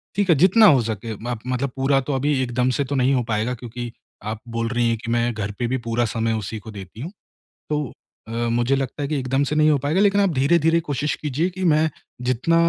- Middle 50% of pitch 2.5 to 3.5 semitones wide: No, average, 4.3 semitones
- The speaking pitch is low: Yes, low, 130 Hz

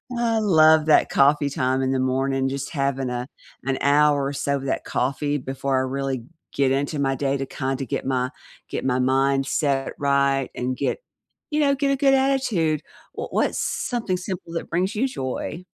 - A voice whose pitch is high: No, medium, 140 Hz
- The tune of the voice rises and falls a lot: No, average, 3.8 semitones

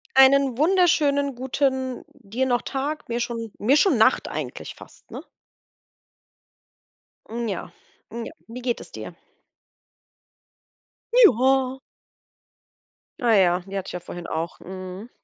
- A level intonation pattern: No, average, 4.2 semitones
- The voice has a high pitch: Yes, very high, 250 Hz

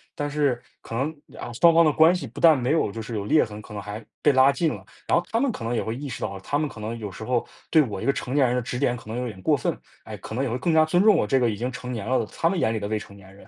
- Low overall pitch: Yes, low, 125 Hz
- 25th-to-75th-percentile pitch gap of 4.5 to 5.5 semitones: Yes, average, 5.1 semitones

